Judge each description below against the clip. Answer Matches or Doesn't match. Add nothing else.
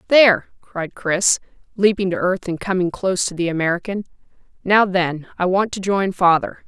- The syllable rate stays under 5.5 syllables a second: Matches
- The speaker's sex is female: Matches